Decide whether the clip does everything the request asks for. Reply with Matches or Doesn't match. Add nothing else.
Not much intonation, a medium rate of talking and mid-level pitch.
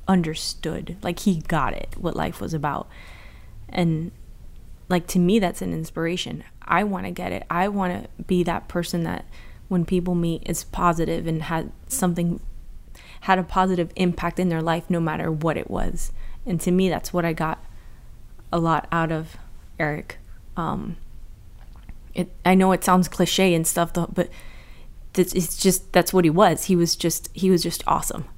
Matches